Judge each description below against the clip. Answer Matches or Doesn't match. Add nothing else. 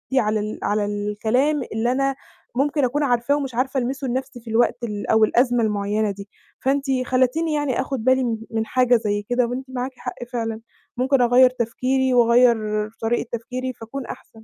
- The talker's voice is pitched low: Doesn't match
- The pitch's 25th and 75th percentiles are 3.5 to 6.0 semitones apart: Doesn't match